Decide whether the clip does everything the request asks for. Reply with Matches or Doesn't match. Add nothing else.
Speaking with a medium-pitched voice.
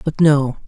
Matches